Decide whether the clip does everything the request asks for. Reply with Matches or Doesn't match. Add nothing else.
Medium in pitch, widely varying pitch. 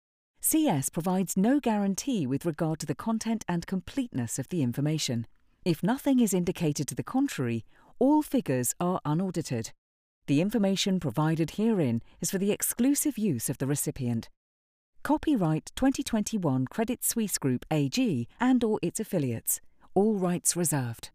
Matches